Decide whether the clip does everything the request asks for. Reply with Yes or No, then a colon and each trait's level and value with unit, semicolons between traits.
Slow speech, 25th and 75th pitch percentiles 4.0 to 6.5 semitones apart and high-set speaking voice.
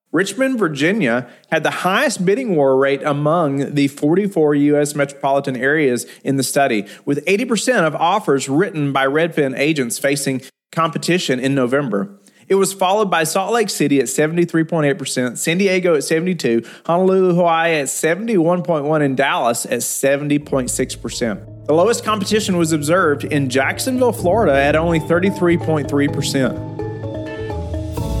No: slow, 130 wpm; average, 4.3 semitones; medium, 145 Hz